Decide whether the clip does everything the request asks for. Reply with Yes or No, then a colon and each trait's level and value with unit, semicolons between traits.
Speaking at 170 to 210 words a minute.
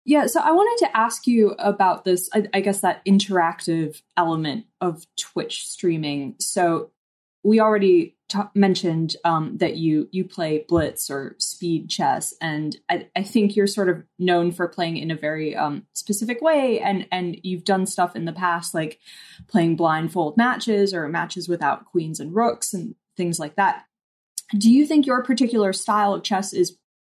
Yes: average, 175 wpm